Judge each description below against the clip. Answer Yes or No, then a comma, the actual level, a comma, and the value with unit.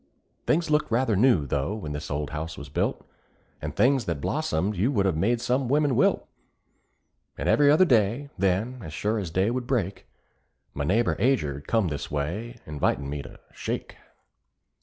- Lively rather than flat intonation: Yes, wide, 8.4 semitones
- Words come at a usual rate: Yes, average, 170 wpm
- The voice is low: Yes, low, 100 Hz